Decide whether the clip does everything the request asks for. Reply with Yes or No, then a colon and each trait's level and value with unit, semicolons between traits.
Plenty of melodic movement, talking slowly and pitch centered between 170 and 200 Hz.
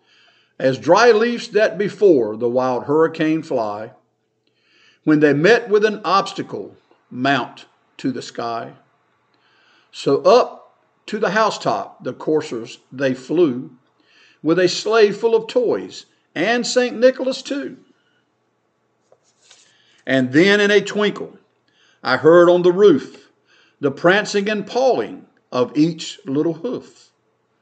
Yes: wide, 6.7 semitones; slow, 120 wpm; medium, 185 Hz